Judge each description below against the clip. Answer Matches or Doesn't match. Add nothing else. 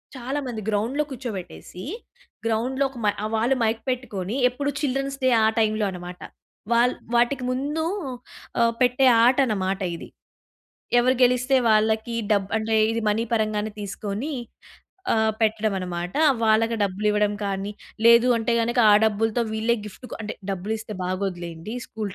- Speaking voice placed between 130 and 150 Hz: Doesn't match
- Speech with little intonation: Doesn't match